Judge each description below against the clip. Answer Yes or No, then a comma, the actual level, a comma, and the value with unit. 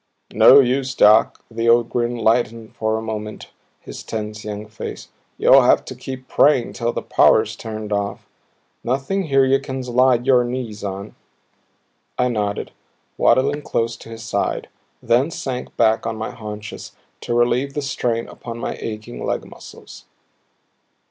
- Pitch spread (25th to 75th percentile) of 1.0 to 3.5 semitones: Yes, average, 2.8 semitones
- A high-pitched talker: No, low, 115 Hz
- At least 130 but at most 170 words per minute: Yes, average, 155 wpm